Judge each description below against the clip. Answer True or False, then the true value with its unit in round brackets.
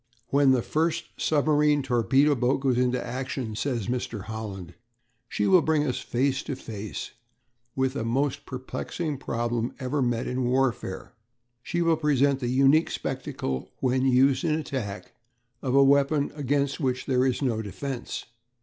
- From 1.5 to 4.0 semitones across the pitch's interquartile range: True (2.8 semitones)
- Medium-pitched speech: False (130 Hz)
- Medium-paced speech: True (150 wpm)